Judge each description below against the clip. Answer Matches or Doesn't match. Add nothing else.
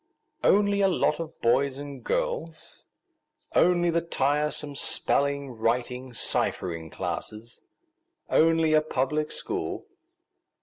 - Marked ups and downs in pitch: Matches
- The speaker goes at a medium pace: Doesn't match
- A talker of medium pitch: Matches